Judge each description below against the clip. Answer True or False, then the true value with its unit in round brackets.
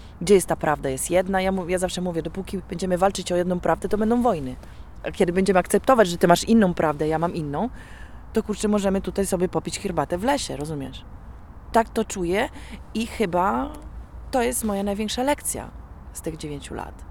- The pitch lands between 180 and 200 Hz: True (190 Hz)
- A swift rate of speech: True (200 wpm)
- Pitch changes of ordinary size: True (3.5 semitones)